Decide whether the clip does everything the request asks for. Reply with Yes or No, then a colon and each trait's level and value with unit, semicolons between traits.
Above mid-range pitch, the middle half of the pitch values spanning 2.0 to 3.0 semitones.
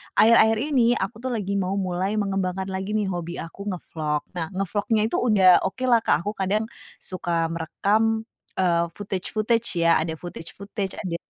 No: high, 195 Hz; average, 3.6 semitones